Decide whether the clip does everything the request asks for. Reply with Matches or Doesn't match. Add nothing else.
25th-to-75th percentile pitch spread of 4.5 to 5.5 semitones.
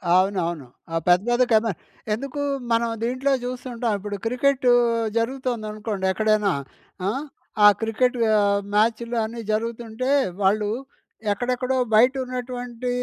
Doesn't match